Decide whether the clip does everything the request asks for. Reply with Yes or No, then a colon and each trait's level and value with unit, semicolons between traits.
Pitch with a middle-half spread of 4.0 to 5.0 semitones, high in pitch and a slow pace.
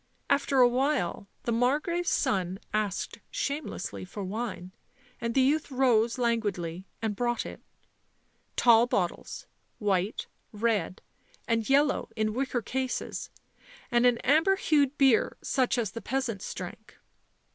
Yes: average, 4.4 semitones; high, 235 Hz; slow, 125 wpm